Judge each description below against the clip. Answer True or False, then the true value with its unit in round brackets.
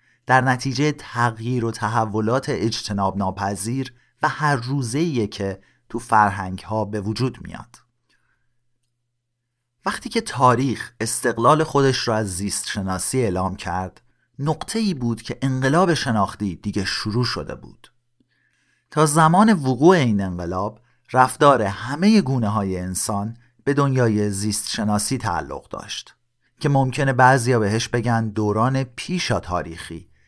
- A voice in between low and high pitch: False (120 Hz)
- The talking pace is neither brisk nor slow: True (125 wpm)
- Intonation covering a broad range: False (4.2 semitones)